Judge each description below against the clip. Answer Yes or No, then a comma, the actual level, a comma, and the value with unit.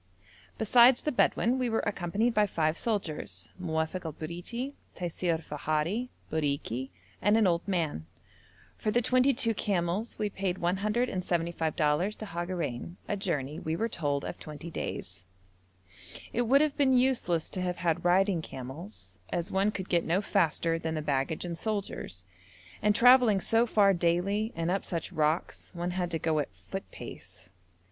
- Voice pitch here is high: No, medium, 180 Hz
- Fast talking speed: No, average, 165 wpm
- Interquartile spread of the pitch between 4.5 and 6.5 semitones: Yes, average, 4.8 semitones